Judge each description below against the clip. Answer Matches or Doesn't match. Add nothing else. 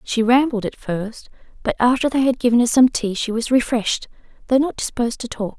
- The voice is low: Doesn't match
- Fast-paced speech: Matches